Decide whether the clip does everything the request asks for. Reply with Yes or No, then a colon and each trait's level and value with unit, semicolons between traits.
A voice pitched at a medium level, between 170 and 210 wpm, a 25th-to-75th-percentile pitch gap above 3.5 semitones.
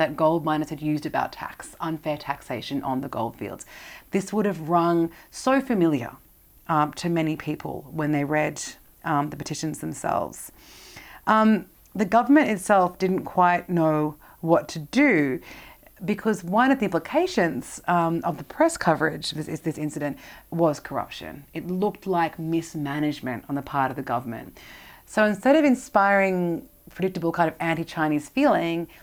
No: medium, 165 Hz; average, 155 wpm; average, 4.3 semitones